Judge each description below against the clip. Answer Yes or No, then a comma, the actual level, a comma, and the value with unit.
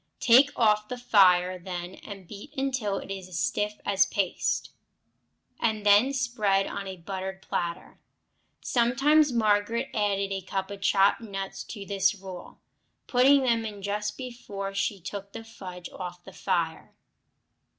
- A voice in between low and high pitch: No, high, 200 Hz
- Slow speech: No, average, 145 wpm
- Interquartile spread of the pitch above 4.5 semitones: No, average, 3.2 semitones